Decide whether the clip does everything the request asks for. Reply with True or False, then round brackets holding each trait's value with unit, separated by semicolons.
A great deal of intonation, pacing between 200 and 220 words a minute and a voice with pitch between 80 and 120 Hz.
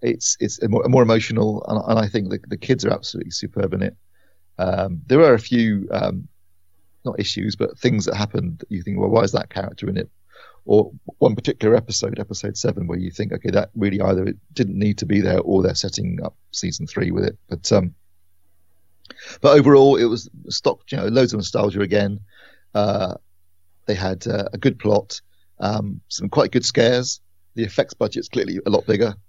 False (3.7 semitones; 205 wpm; 100 Hz)